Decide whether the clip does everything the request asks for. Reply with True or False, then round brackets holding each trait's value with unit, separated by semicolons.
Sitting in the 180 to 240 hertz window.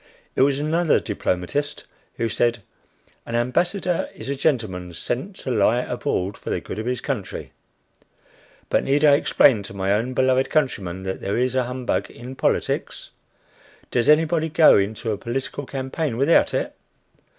False (125 Hz)